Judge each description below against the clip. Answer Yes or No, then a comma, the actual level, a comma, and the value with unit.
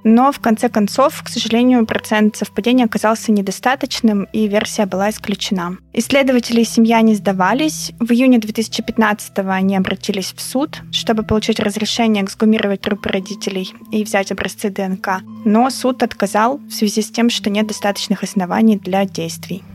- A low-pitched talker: No, high, 215 Hz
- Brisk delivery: No, average, 150 wpm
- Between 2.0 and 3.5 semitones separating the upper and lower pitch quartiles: Yes, narrow, 2.6 semitones